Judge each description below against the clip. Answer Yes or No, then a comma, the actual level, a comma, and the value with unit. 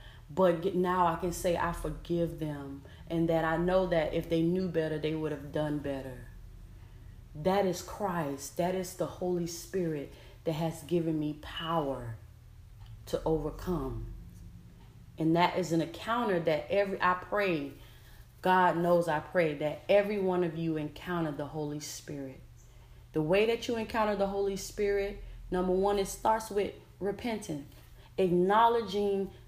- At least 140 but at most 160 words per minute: Yes, average, 150 wpm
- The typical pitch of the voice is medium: Yes, medium, 165 Hz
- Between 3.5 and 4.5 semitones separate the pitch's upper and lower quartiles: Yes, average, 4.1 semitones